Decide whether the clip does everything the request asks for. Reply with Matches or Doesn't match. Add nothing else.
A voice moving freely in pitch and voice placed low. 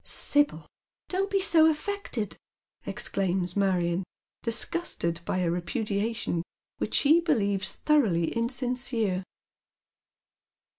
Doesn't match